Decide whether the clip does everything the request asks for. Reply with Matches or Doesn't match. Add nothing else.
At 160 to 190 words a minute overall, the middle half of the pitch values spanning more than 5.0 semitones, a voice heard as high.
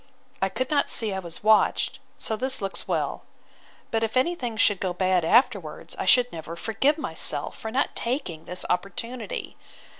Matches